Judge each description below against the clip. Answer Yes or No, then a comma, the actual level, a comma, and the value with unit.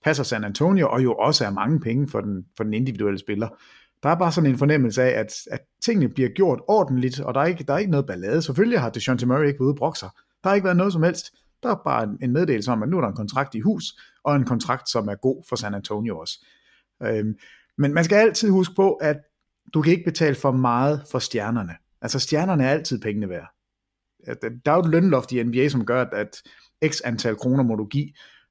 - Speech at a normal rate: No, fast, 240 wpm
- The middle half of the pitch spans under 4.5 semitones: No, average, 5.0 semitones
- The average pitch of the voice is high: No, low, 135 Hz